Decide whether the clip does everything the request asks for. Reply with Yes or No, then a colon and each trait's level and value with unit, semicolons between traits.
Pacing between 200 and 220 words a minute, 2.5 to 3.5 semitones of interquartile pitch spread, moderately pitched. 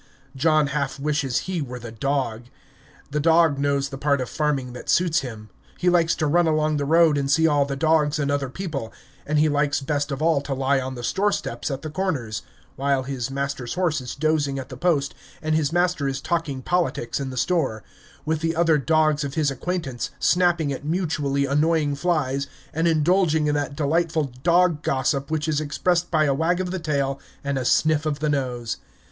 Yes: fast, 205 wpm; average, 2.9 semitones; medium, 150 Hz